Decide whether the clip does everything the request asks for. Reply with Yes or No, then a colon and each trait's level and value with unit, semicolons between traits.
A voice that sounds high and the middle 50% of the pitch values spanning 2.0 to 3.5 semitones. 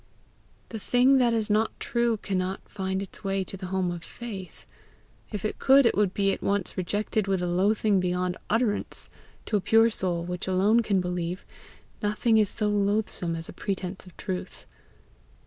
Yes: high, 195 Hz; average, 2.9 semitones